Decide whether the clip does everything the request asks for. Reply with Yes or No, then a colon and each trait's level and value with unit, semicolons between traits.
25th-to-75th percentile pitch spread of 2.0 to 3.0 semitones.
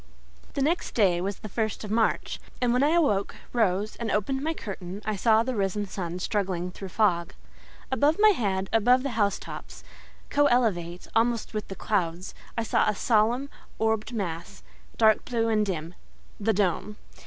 No: average, 3.7 semitones